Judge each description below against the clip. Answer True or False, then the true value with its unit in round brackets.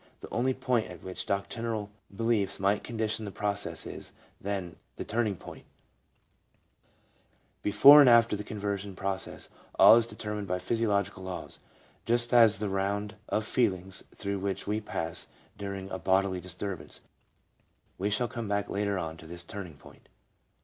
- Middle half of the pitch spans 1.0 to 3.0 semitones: True (2.6 semitones)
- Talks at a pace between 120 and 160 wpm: True (155 wpm)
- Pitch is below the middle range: True (100 Hz)